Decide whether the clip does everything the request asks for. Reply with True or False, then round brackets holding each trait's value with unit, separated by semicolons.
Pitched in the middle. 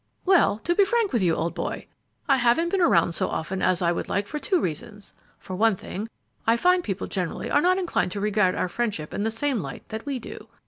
False (220 Hz)